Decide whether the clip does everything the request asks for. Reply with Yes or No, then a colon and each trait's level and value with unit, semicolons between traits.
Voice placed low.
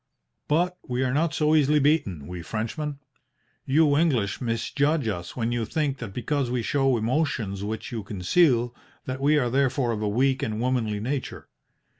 Yes: low, 125 Hz